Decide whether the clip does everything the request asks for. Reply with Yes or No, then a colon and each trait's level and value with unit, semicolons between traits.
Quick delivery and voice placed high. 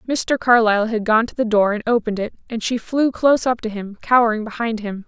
Yes: fast, 235 wpm; high, 225 Hz